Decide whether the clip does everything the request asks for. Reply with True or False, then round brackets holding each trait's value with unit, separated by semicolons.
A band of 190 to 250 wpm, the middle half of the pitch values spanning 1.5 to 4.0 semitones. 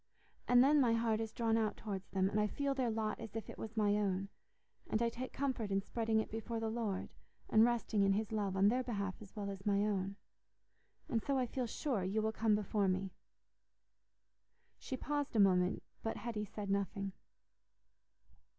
True (195 wpm; 2.6 semitones)